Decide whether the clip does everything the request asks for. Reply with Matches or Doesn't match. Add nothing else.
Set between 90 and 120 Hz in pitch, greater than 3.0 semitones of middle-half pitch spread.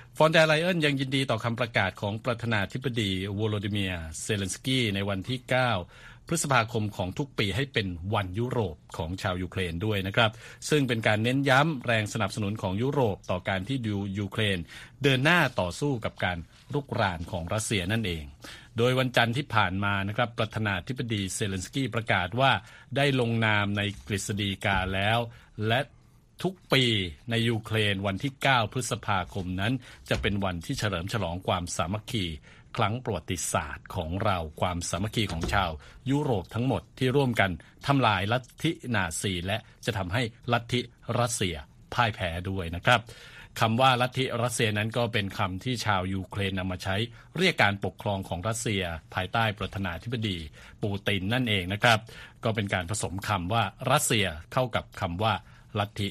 Matches